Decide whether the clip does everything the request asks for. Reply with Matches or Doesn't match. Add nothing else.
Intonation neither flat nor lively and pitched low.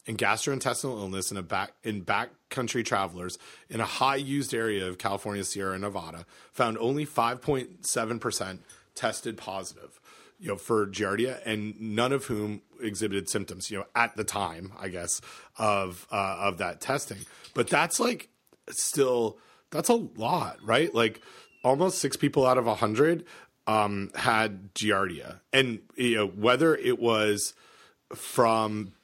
Matches